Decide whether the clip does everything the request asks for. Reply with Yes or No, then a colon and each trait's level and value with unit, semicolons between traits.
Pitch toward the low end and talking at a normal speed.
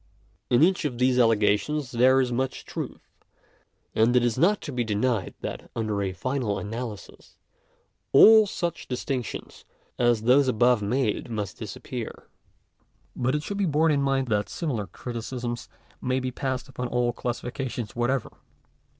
Yes: low, 125 Hz; average, 150 wpm